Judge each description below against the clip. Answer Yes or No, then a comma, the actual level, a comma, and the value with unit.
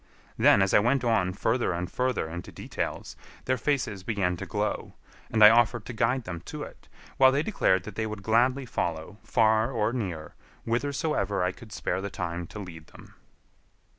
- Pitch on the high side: No, low, 110 Hz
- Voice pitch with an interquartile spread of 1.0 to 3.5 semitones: No, average, 4.9 semitones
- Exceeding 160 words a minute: Yes, average, 185 wpm